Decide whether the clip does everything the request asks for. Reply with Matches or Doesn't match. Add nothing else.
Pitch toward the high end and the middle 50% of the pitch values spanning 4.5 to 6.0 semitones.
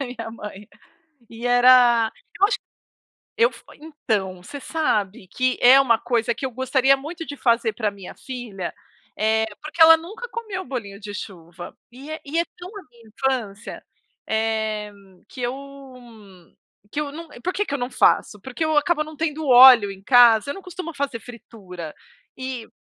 Matches